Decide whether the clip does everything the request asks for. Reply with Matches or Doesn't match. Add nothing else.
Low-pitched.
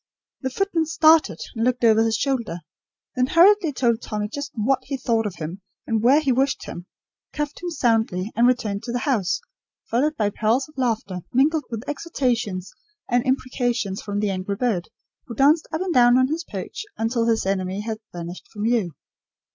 Doesn't match